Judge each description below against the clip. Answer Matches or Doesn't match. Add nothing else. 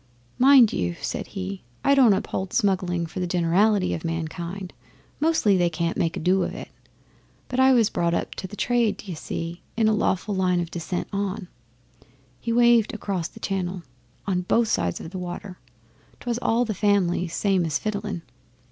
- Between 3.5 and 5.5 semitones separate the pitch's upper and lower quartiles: Matches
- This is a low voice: Doesn't match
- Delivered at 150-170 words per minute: Doesn't match